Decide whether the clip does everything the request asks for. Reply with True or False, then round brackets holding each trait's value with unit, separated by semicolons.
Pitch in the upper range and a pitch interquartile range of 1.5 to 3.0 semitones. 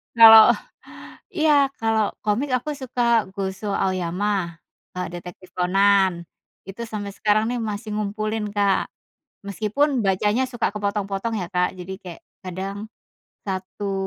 True (205 Hz; 2.7 semitones)